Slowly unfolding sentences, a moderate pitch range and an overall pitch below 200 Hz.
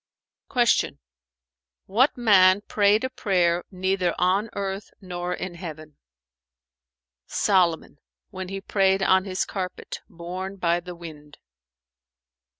No: slow, 110 wpm; narrow, 2.1 semitones; medium, 185 Hz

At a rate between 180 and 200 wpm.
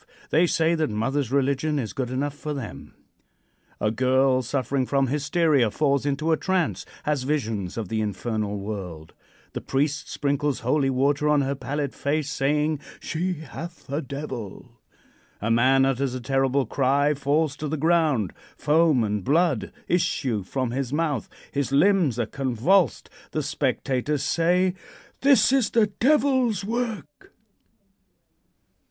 No: average, 140 wpm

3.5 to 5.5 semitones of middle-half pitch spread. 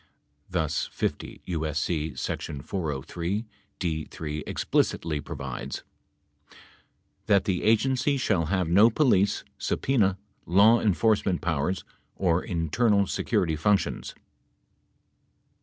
Yes: average, 4.5 semitones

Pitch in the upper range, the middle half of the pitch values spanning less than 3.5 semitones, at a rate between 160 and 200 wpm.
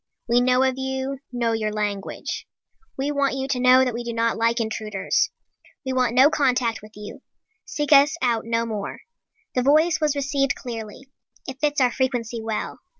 Yes: very high, 250 Hz; average, 2.9 semitones; average, 180 wpm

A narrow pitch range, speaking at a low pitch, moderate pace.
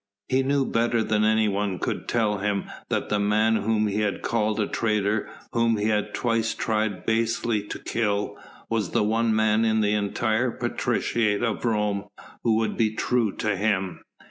Yes: narrow, 1.6 semitones; low, 110 Hz; average, 170 wpm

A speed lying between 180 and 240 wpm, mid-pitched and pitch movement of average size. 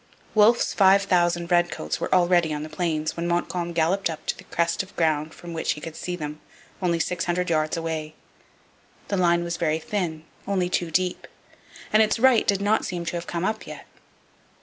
No: average, 195 wpm; medium, 175 Hz; narrow, 2.2 semitones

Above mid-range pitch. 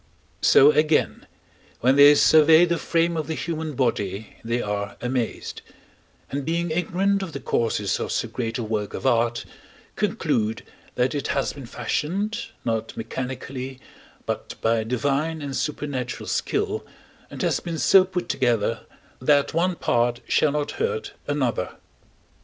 No: medium, 140 Hz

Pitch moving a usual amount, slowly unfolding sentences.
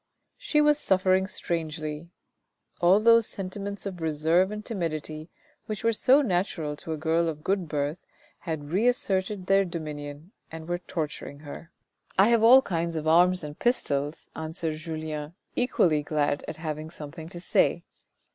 No: average, 3.9 semitones; average, 155 wpm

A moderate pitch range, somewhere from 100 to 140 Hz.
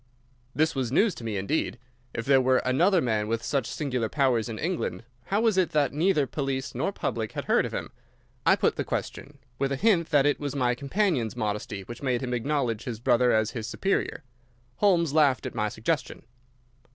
Yes: average, 4.8 semitones; low, 135 Hz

